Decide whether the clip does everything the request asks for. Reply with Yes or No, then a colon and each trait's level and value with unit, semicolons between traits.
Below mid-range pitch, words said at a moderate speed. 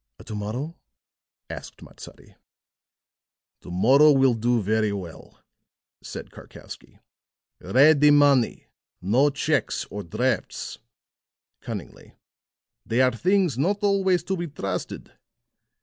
No: low, 130 Hz; slow, 100 wpm